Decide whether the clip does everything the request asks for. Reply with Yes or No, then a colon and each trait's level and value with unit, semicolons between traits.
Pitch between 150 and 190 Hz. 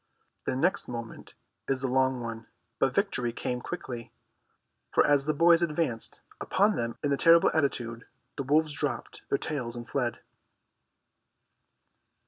No: low, 135 Hz